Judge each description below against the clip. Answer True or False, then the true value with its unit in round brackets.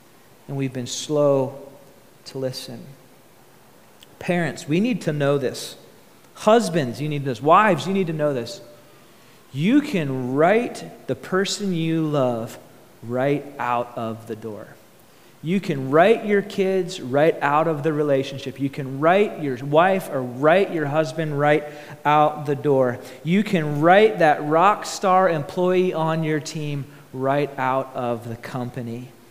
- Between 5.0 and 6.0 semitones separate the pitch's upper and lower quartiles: False (4.3 semitones)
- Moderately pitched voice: True (150 Hz)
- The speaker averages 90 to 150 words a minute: True (145 wpm)